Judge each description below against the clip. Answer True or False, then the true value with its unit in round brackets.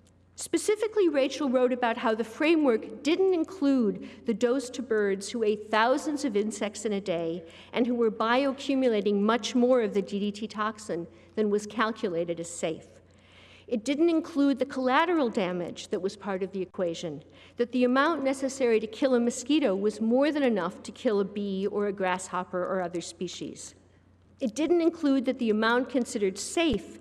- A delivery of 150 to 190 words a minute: True (175 wpm)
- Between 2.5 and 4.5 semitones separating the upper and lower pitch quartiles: False (5.2 semitones)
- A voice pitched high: True (225 Hz)